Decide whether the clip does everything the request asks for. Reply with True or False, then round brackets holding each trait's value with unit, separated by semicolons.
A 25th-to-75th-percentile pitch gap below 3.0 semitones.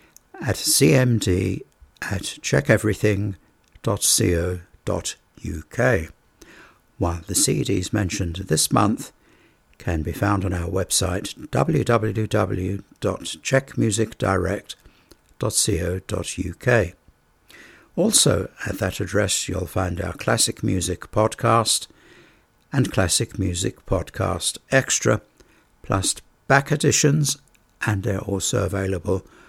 False (3.4 semitones)